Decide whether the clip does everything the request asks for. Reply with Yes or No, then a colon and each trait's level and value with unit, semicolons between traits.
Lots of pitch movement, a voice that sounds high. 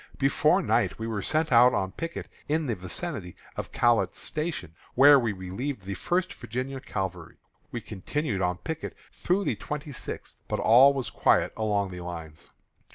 No: wide, 7.5 semitones; low, 115 Hz